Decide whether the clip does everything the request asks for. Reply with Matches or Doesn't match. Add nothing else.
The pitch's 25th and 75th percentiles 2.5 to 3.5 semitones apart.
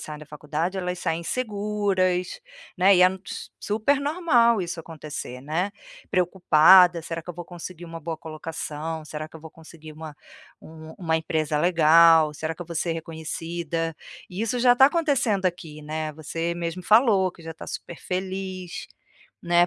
Matches